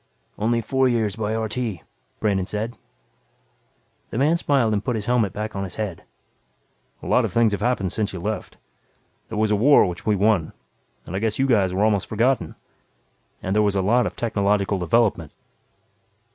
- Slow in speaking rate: No, average, 185 wpm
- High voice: No, low, 105 Hz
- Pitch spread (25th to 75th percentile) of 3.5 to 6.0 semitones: No, average, 2.8 semitones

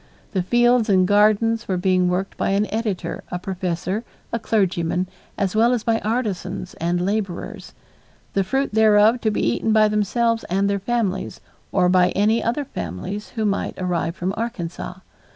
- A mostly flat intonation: No, average, 3.5 semitones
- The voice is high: Yes, high, 200 Hz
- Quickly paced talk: No, average, 165 wpm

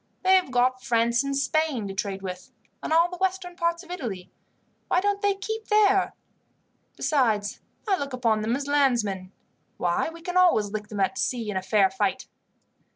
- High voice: Yes, very high, 260 Hz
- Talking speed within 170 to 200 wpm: Yes, average, 185 wpm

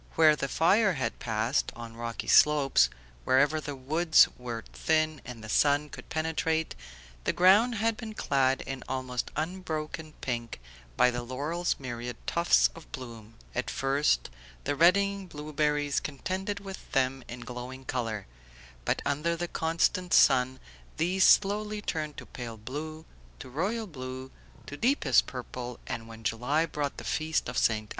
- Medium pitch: Yes, medium, 145 Hz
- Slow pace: No, average, 150 wpm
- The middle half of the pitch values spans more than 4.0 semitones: Yes, average, 4.8 semitones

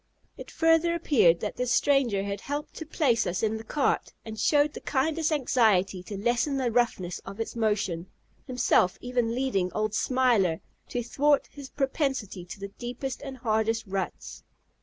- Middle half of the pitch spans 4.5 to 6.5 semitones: Yes, average, 5.2 semitones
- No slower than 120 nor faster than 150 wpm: No, average, 165 wpm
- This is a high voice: Yes, high, 240 Hz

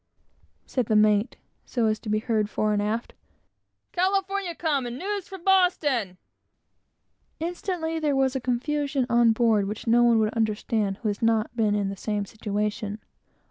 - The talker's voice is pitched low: No, high, 230 Hz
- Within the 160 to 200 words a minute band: Yes, average, 170 wpm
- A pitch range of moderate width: No, wide, 5.9 semitones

